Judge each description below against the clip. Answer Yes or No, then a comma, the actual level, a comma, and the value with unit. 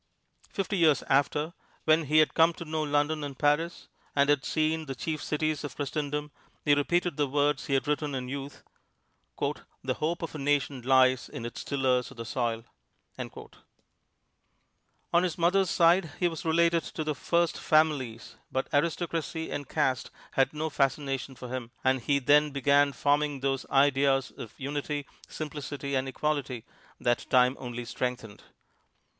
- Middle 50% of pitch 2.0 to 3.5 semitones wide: Yes, average, 2.7 semitones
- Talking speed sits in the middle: Yes, average, 160 wpm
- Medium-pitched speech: Yes, medium, 145 Hz